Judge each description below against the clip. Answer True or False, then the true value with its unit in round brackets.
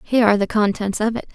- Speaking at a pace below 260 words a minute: False (265 wpm)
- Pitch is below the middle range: False (215 Hz)